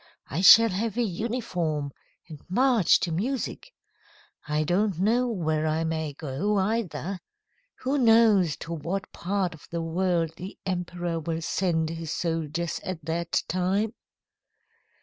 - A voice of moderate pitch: Yes, medium, 175 Hz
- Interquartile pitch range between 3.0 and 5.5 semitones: Yes, average, 4.2 semitones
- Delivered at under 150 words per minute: Yes, slow, 135 wpm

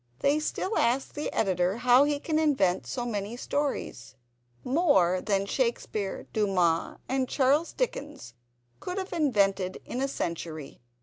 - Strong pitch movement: Yes, wide, 7.7 semitones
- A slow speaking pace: Yes, slow, 130 wpm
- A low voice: No, high, 230 Hz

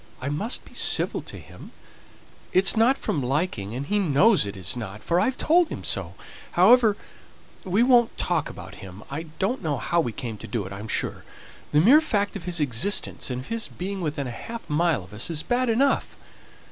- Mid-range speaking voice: Yes, medium, 170 Hz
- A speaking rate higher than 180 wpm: Yes, average, 200 wpm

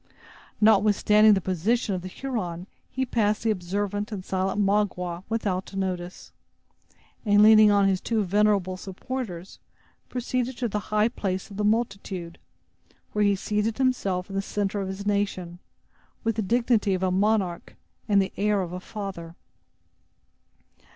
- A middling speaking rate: Yes, average, 150 wpm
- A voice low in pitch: No, high, 205 Hz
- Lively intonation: No, narrow, 2.5 semitones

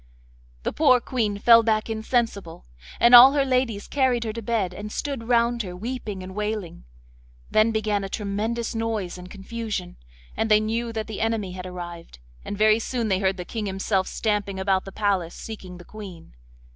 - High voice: Yes, high, 215 Hz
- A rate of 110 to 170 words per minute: No, average, 185 wpm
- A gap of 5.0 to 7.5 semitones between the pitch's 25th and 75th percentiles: No, average, 3.2 semitones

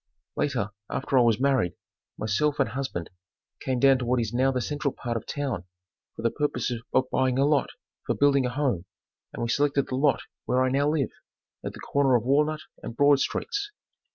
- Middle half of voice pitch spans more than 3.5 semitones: No, average, 2.9 semitones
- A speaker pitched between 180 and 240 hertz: No, low, 130 Hz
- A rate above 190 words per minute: Yes, average, 200 wpm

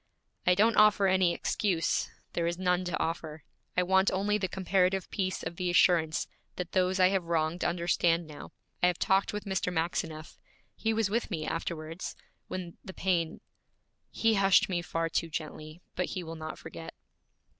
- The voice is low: No, medium, 180 Hz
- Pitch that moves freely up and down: No, narrow, 2.4 semitones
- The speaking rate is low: No, average, 175 wpm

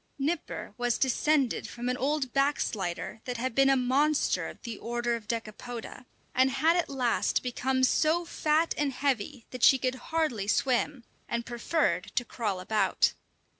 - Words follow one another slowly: No, average, 160 wpm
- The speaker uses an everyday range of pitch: Yes, average, 3.2 semitones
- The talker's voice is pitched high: Yes, very high, 255 Hz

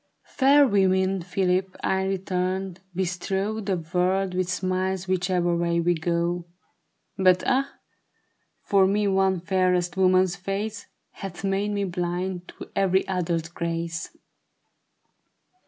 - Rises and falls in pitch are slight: Yes, narrow, 1.5 semitones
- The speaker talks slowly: Yes, slow, 115 wpm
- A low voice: No, medium, 185 Hz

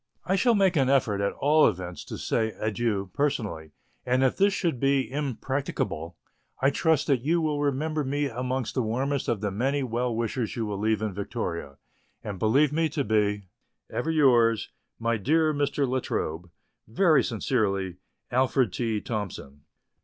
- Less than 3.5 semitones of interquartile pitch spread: No, average, 5.3 semitones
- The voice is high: No, low, 125 Hz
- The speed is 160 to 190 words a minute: Yes, average, 165 wpm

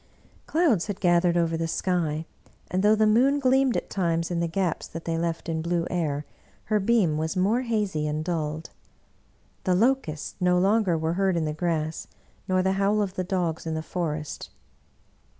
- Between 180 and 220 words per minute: Yes, average, 185 wpm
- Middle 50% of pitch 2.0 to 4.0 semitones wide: Yes, average, 3.7 semitones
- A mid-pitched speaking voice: Yes, medium, 175 Hz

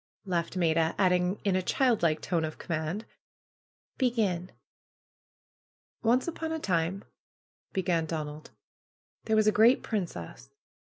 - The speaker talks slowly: Yes, slow, 120 wpm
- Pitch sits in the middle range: Yes, medium, 180 Hz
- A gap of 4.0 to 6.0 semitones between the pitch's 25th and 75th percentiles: Yes, average, 4.8 semitones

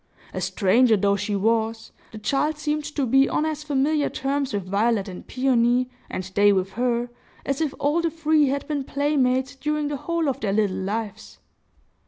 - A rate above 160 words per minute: Yes, average, 185 wpm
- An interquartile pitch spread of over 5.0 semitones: Yes, wide, 5.4 semitones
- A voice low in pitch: No, very high, 260 Hz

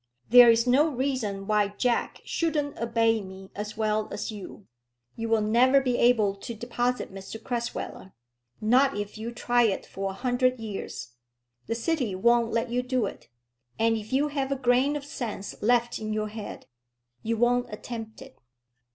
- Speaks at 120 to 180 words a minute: Yes, average, 170 wpm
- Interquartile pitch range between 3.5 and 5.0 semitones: No, average, 2.8 semitones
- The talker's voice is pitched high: Yes, high, 230 Hz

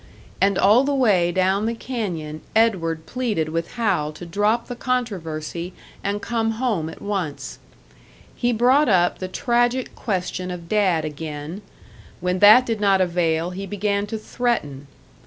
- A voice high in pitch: Yes, high, 195 Hz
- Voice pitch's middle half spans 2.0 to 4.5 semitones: No, average, 5.3 semitones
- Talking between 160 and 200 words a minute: No, average, 150 wpm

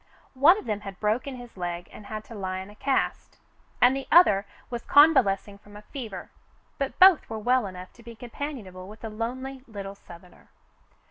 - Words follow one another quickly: No, average, 195 wpm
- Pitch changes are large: No, average, 4.8 semitones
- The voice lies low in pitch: No, high, 220 Hz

